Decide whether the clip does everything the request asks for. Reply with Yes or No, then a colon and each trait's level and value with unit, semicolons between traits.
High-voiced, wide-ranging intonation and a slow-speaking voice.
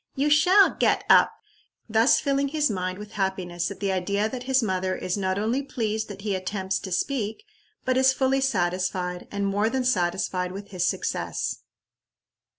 No: high, 205 Hz; wide, 5.7 semitones; average, 170 wpm